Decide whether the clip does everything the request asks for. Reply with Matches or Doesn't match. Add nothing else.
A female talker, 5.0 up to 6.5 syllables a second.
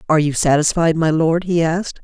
Matches